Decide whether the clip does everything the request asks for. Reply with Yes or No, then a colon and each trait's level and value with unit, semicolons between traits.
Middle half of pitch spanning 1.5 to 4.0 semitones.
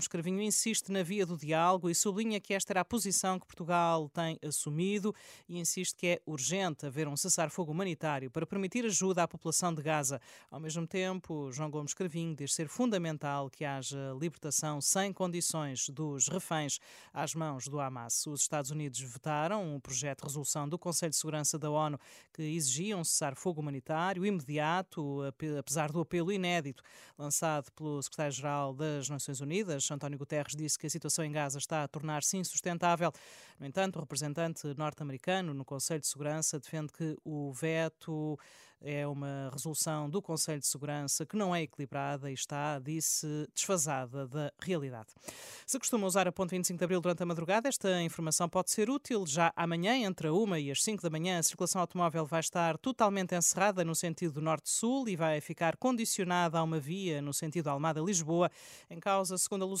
Yes: average, 3.6 semitones